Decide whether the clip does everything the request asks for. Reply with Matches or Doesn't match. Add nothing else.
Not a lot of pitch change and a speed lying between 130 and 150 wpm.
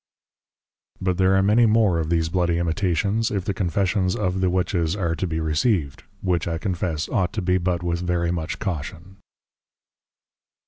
Doesn't match